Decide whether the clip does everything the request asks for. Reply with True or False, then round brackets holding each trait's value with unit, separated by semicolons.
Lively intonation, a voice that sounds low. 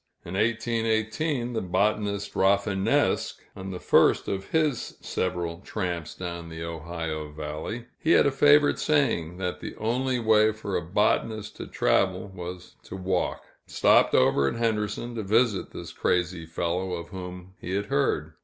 False (4.2 semitones; 95 Hz)